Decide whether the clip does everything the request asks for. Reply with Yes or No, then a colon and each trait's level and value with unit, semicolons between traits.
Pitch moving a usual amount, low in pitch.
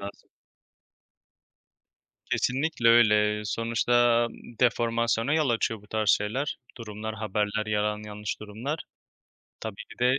No: narrow, 2.3 semitones; low, 110 Hz